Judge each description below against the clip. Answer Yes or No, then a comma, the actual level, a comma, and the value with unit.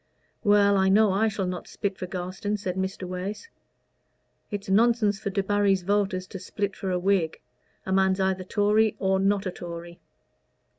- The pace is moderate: Yes, average, 170 wpm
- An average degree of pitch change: No, narrow, 1.6 semitones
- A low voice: No, high, 195 Hz